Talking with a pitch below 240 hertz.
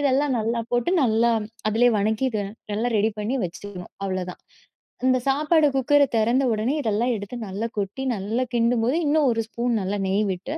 Yes: high, 230 Hz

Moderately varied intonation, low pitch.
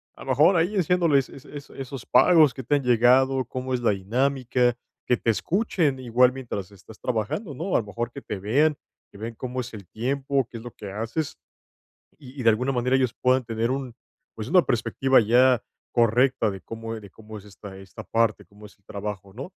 Yes: average, 3.5 semitones; low, 125 Hz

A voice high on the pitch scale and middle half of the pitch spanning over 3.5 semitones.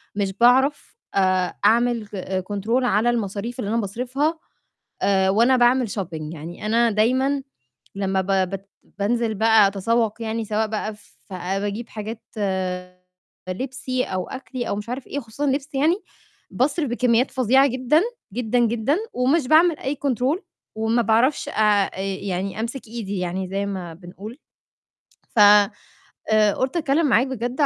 Yes: high, 225 Hz; average, 4.3 semitones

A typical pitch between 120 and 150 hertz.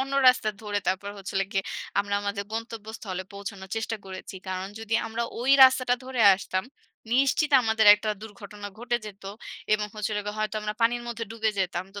No: high, 215 Hz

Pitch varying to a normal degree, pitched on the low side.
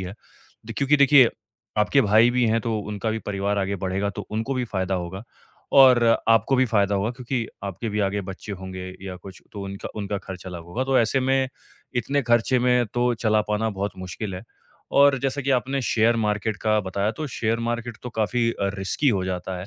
Yes: average, 4.0 semitones; low, 110 Hz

